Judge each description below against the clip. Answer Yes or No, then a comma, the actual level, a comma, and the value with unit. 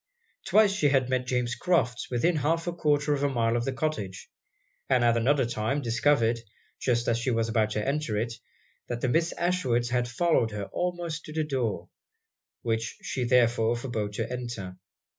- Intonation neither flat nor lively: Yes, average, 4.0 semitones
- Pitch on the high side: No, low, 125 Hz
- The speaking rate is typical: Yes, average, 180 wpm